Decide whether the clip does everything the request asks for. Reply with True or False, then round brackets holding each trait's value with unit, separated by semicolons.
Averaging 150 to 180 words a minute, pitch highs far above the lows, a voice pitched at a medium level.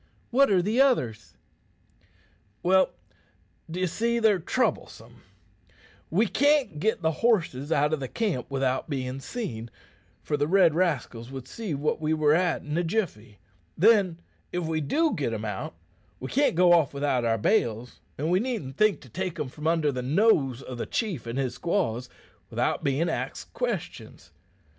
True (165 wpm; 6.7 semitones; 155 Hz)